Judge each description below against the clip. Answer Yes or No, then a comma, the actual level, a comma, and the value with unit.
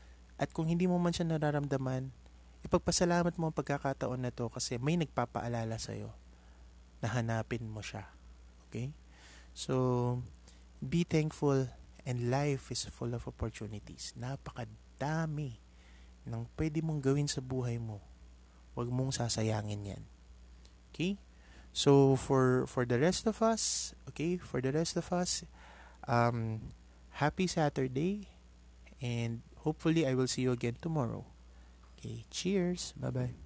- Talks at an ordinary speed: Yes, average, 130 wpm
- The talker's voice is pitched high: No, low, 120 Hz